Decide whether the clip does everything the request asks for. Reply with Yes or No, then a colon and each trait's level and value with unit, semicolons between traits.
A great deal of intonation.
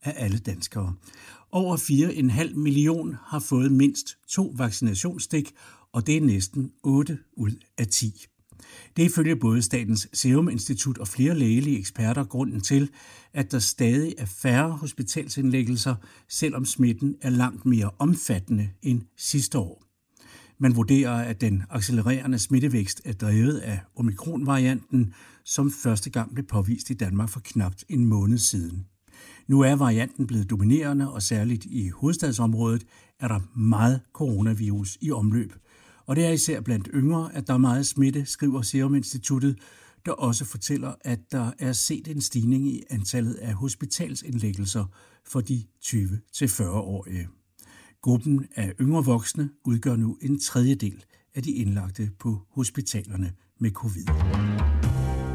No: average, 4.4 semitones